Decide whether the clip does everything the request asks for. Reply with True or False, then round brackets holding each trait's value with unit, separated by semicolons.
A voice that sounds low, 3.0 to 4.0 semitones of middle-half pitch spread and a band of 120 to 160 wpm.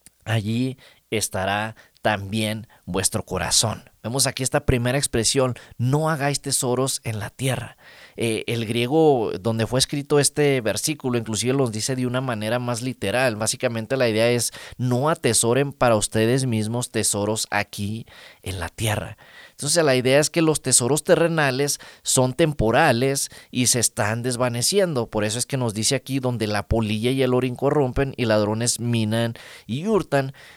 True (125 Hz; 3.6 semitones; 155 wpm)